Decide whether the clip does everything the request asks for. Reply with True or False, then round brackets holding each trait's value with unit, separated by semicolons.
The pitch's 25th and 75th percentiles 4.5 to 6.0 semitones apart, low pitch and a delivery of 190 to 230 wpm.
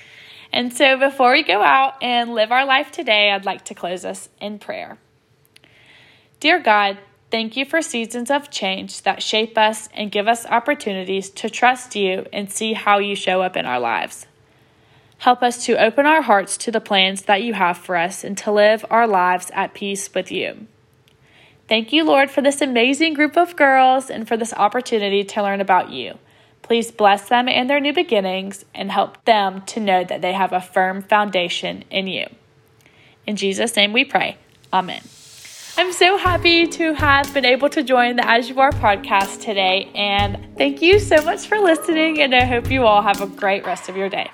False (5.4 semitones; 215 Hz; 195 wpm)